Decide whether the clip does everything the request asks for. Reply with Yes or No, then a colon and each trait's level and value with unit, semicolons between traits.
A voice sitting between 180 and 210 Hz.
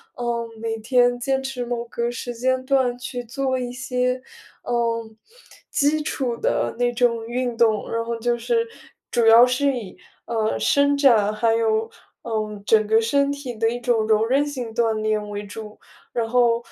No: high, 240 Hz